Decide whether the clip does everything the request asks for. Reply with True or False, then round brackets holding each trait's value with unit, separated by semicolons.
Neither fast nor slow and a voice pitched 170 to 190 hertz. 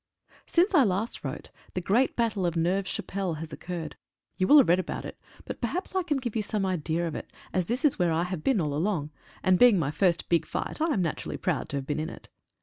False (250 wpm; 185 Hz)